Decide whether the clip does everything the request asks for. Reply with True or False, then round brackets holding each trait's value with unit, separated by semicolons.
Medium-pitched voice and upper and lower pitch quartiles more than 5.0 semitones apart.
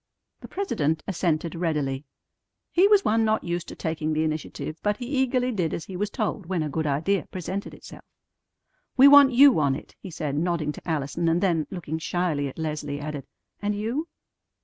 True (170 Hz; 5.4 semitones)